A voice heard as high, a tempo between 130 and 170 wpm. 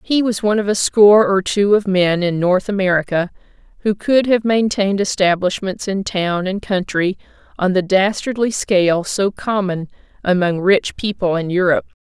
Yes: high, 195 Hz; average, 165 wpm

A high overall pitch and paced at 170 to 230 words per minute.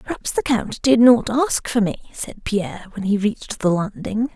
Yes: high, 225 Hz; fast, 205 wpm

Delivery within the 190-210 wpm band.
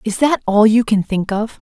No: fast, 240 wpm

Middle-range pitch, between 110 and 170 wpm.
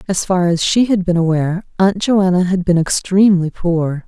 No: medium, 180 Hz; average, 190 wpm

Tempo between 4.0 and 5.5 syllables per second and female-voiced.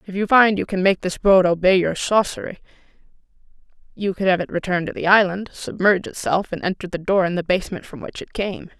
No: 6.0 syllables/s; female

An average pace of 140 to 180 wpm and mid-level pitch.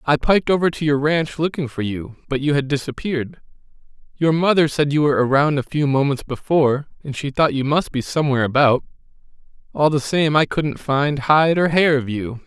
No: average, 200 wpm; medium, 145 Hz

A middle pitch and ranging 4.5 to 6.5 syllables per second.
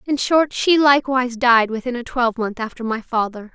No: high, 245 Hz; 5.5 syllables/s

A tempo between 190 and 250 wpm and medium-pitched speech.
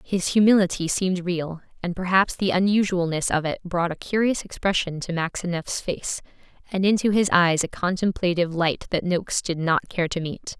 No: average, 175 wpm; medium, 180 Hz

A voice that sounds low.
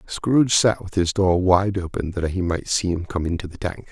Yes: very low, 90 Hz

